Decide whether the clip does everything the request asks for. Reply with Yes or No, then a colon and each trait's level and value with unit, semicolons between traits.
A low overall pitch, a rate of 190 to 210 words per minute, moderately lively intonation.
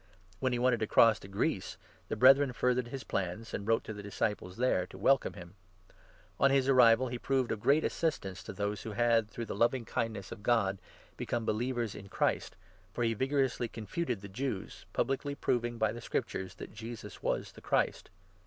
Yes: low, 115 Hz; average, 200 wpm; average, 3.7 semitones